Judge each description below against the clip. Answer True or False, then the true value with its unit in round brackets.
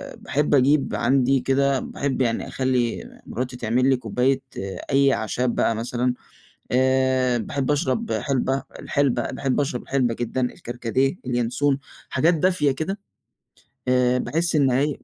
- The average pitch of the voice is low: True (130 Hz)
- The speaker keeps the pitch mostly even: True (2.0 semitones)